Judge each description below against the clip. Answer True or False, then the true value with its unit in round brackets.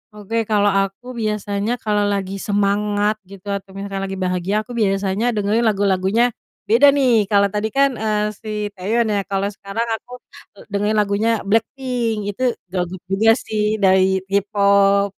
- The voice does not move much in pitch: True (1.8 semitones)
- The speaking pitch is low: False (205 Hz)